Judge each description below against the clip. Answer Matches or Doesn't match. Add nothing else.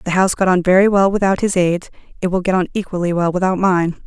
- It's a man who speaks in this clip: Doesn't match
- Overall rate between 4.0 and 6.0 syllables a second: Doesn't match